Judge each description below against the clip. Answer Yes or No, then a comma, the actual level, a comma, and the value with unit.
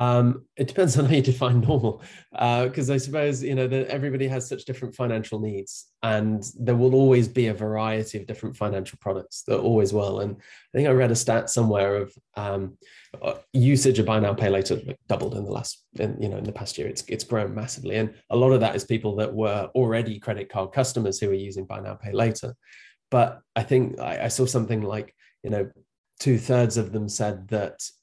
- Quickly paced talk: Yes, fast, 220 wpm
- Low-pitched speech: Yes, low, 115 Hz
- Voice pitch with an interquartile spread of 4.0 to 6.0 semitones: No, average, 3.3 semitones